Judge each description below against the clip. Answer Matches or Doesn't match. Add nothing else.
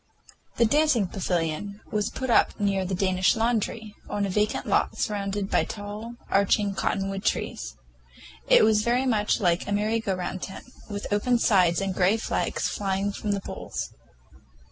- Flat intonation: Matches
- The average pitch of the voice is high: Matches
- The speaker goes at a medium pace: Matches